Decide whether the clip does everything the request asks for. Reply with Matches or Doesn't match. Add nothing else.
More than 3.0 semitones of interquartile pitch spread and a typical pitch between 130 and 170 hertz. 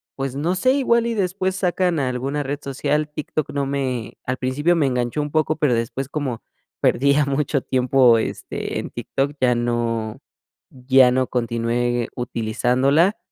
Matches